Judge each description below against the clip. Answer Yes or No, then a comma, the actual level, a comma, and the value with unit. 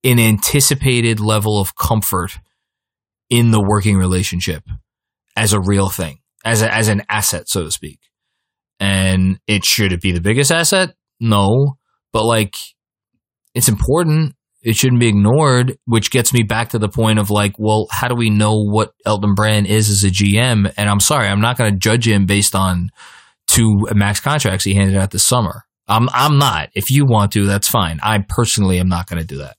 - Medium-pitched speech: No, low, 105 Hz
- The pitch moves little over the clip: No, average, 3.0 semitones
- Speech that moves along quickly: No, average, 195 wpm